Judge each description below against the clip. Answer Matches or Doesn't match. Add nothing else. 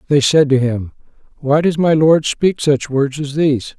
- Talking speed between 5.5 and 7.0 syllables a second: Doesn't match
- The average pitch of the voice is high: Doesn't match